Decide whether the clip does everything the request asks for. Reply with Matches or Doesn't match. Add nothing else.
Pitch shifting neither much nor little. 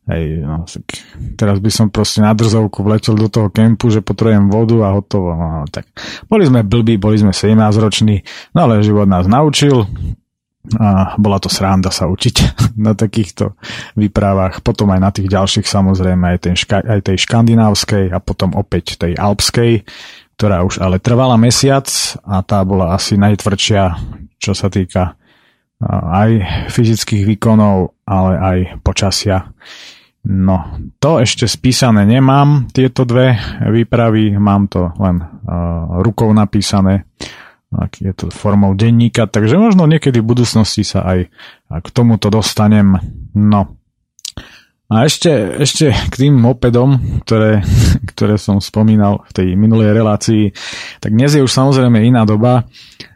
Matches